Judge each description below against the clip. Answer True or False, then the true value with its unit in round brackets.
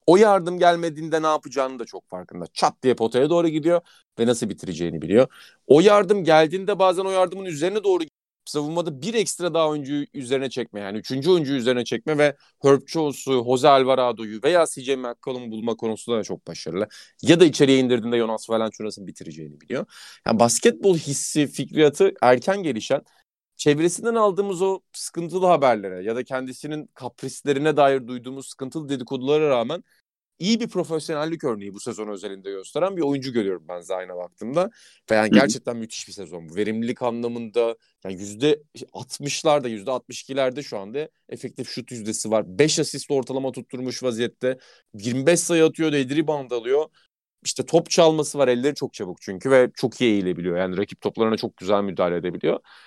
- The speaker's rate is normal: False (160 wpm)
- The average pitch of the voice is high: False (135 Hz)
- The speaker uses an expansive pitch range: True (5.7 semitones)